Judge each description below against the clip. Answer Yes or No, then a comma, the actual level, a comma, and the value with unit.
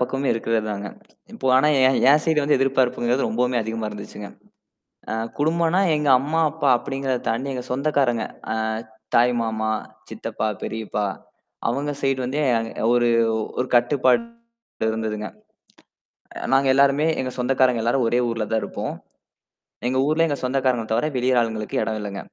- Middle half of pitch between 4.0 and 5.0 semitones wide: No, average, 3.5 semitones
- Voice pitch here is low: Yes, low, 125 Hz